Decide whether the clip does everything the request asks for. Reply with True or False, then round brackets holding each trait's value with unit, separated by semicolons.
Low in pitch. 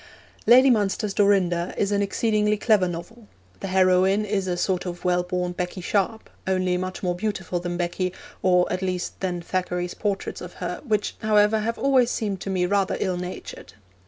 False (190 Hz)